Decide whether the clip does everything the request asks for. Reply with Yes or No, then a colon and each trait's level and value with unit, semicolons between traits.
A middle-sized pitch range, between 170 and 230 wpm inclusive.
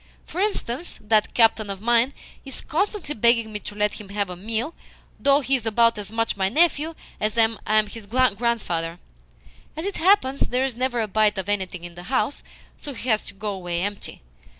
Yes: average, 4.2 semitones; average, 200 wpm